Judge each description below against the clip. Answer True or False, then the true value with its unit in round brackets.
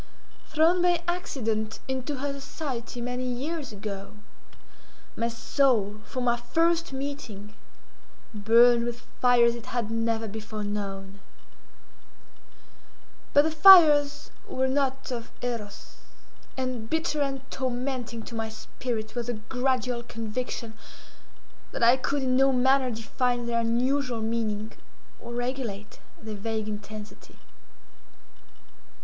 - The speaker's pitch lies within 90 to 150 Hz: False (245 Hz)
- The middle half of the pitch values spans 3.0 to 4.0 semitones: True (3.3 semitones)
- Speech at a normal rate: False (115 wpm)